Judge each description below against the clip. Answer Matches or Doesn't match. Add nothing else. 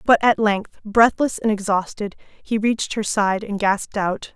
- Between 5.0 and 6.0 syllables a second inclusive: Doesn't match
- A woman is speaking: Matches